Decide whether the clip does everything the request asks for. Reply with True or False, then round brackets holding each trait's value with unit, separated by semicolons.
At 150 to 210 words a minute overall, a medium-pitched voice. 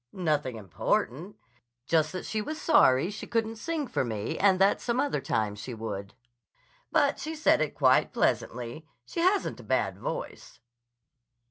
True (155 wpm; 170 Hz)